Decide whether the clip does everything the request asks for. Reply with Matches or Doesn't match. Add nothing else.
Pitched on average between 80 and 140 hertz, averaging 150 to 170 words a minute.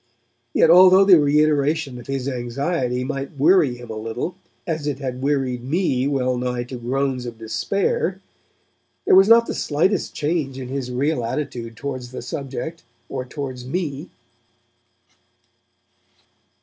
Doesn't match